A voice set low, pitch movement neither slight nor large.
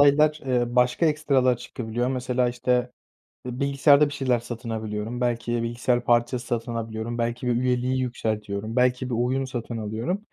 No: low, 125 Hz; narrow, 1.6 semitones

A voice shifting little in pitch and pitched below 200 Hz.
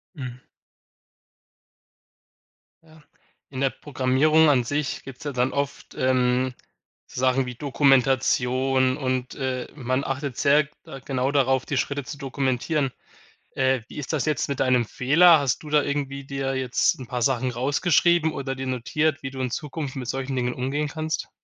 Yes: narrow, 2.0 semitones; low, 135 Hz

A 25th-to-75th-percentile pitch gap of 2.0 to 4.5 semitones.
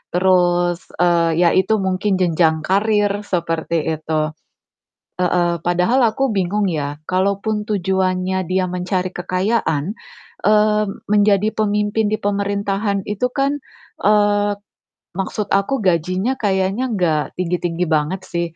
Yes: average, 2.9 semitones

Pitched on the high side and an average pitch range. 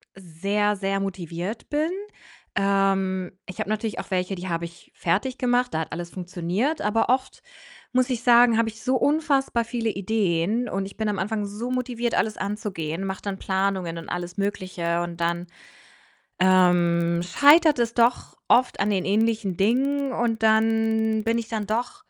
Yes: high, 205 Hz; average, 4.2 semitones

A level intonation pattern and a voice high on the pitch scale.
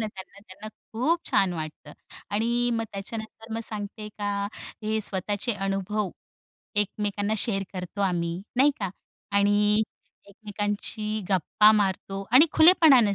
Yes: narrow, 2.1 semitones; high, 210 Hz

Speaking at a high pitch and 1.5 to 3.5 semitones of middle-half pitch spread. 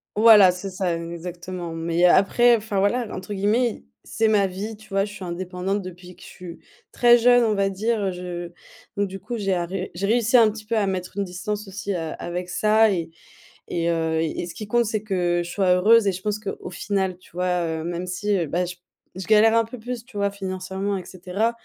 Yes: high, 195 Hz; average, 3.0 semitones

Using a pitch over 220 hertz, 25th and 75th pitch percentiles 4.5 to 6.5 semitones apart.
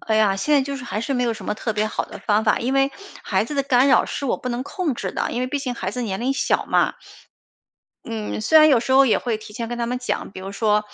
No: high, 240 Hz; average, 3.9 semitones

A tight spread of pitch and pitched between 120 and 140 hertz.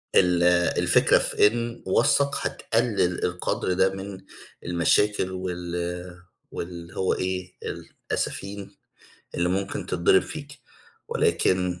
No: narrow, 2.3 semitones; very low, 95 Hz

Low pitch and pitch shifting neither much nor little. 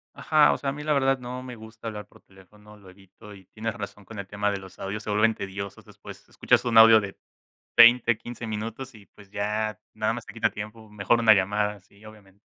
No: low, 105 Hz; narrow, 2.2 semitones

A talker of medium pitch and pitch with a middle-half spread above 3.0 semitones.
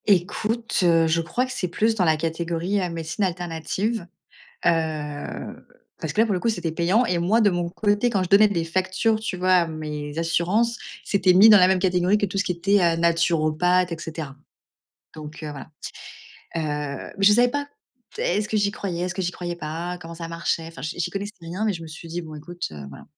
Yes: medium, 175 Hz; average, 3.5 semitones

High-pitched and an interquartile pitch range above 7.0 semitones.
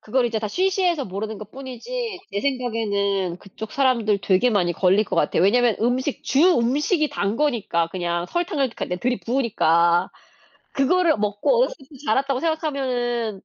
No: high, 240 Hz; wide, 5.6 semitones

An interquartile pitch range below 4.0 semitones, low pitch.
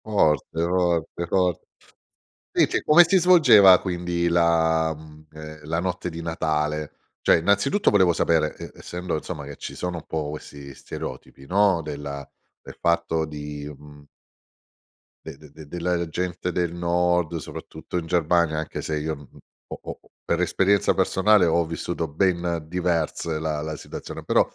Yes: narrow, 2.5 semitones; very low, 85 Hz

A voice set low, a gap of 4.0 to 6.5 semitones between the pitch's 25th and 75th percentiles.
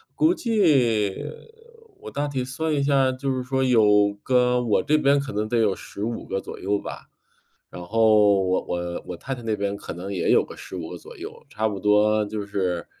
Yes: low, 110 Hz; average, 4.8 semitones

